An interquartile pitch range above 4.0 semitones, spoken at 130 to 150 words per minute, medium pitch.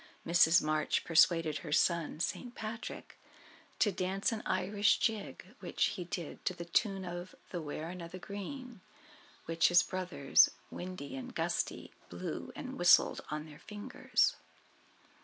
No: average, 3.7 semitones; average, 140 wpm; medium, 180 Hz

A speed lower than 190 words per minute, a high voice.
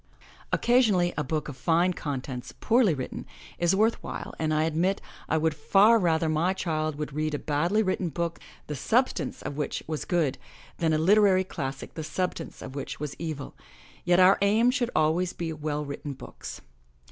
No: average, 180 wpm; medium, 160 Hz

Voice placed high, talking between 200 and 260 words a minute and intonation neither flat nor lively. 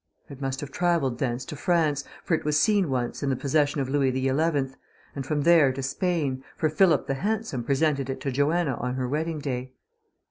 No: medium, 140 Hz; fast, 205 wpm; average, 3.2 semitones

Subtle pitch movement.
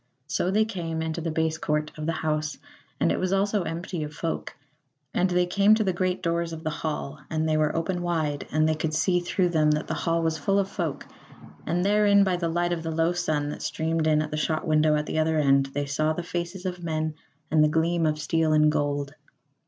Yes: narrow, 2.3 semitones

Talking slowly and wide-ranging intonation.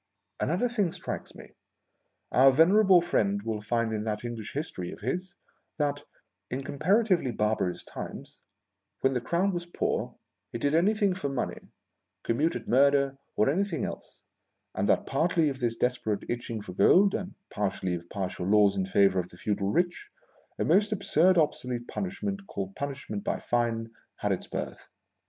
No: average, 165 wpm; wide, 8.5 semitones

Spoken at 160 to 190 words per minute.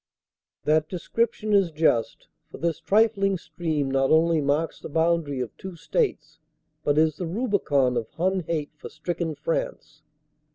No: average, 150 wpm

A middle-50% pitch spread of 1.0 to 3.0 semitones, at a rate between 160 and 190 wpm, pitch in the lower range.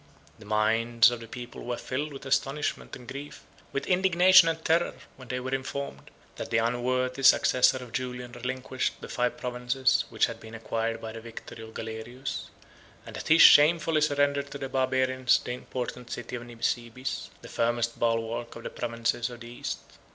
Yes: narrow, 2.5 semitones; average, 180 wpm; low, 125 Hz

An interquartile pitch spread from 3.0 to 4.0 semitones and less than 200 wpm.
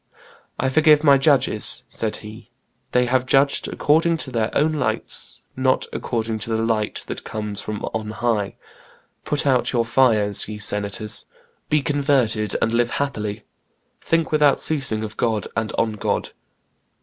No: average, 4.5 semitones; average, 150 wpm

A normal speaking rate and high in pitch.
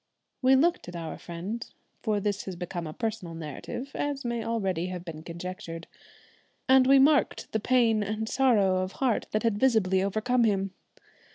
Yes: average, 170 wpm; high, 210 Hz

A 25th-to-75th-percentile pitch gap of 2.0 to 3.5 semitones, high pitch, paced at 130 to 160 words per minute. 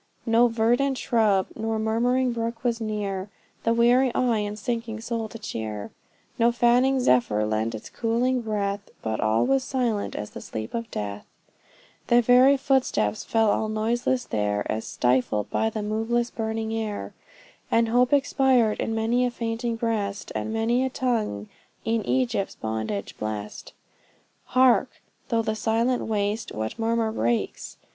Yes: average, 3.0 semitones; high, 225 Hz; average, 150 wpm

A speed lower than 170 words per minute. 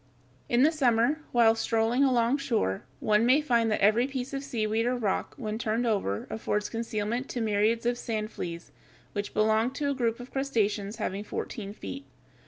No: average, 180 wpm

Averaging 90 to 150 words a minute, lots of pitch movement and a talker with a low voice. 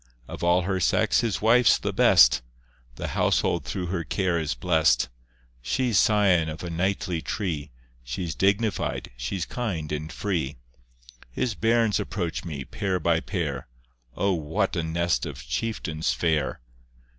No: average, 145 wpm; average, 4.2 semitones; very low, 85 Hz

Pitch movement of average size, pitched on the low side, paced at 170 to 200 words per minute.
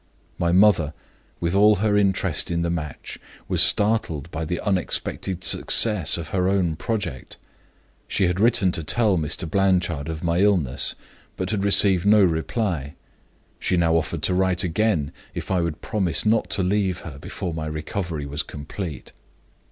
No: average, 3.6 semitones; very low, 90 Hz; average, 160 wpm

